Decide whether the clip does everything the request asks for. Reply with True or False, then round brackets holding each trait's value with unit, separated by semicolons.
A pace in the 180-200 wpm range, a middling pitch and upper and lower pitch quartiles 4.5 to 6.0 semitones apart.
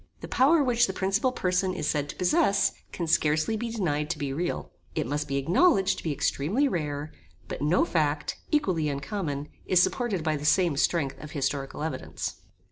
True (185 wpm; 165 Hz; 5.1 semitones)